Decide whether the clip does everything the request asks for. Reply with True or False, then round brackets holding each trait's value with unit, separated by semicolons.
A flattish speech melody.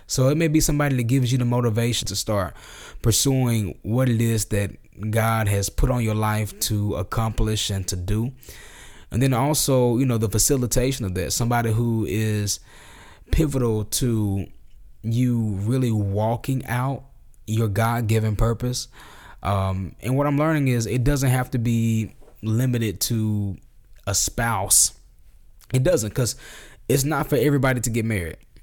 False (3.3 semitones)